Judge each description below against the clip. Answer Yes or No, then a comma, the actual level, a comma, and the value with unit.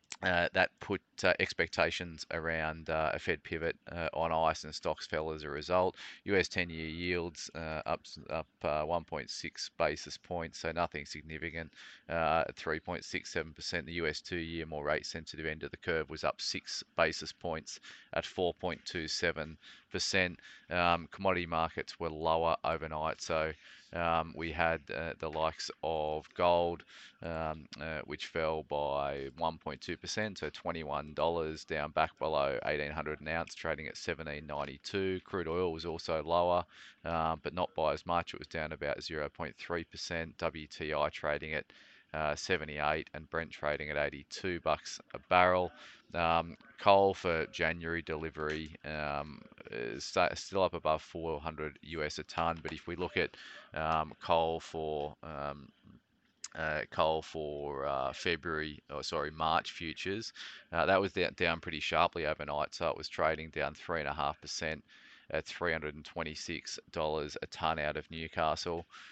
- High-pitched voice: No, very low, 80 Hz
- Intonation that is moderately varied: No, narrow, 1.6 semitones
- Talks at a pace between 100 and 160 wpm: Yes, average, 150 wpm